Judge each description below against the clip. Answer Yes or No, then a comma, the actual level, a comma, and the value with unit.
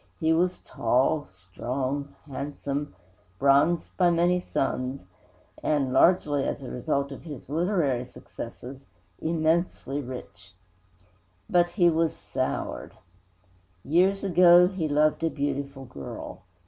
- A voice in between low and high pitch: Yes, medium, 145 Hz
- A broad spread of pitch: No, average, 4.1 semitones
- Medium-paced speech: No, slow, 110 wpm